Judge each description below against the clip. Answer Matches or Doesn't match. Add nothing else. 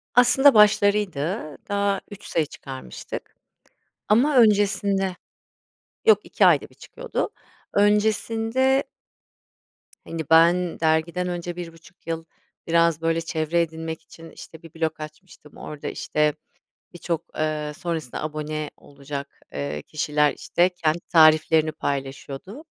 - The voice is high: Doesn't match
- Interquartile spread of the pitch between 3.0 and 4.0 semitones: Doesn't match